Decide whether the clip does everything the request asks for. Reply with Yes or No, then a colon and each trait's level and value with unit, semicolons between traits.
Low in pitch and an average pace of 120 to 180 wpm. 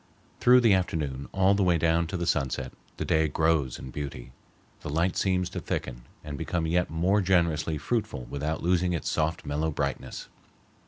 Yes: very low, 80 Hz; average, 175 wpm